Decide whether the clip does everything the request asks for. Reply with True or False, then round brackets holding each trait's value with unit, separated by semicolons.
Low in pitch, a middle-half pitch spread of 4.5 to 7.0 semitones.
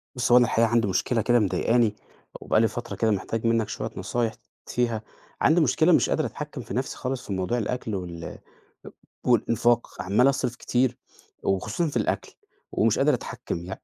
False (115 Hz; 2.9 semitones)